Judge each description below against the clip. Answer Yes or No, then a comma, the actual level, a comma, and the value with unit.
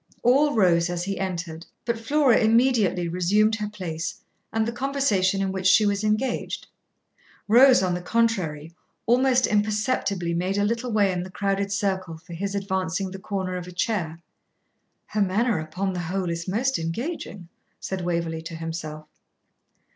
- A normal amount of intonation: Yes, average, 4.0 semitones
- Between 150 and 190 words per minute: Yes, average, 160 wpm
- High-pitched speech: Yes, high, 195 Hz